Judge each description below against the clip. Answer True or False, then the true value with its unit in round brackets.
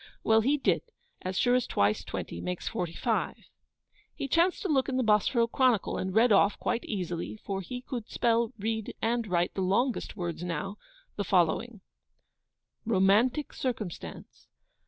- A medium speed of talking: True (155 wpm)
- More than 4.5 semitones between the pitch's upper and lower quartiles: True (4.9 semitones)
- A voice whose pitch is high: True (220 Hz)